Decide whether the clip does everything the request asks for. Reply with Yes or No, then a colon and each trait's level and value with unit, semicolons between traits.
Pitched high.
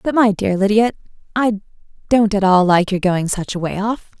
Yes: high, 205 Hz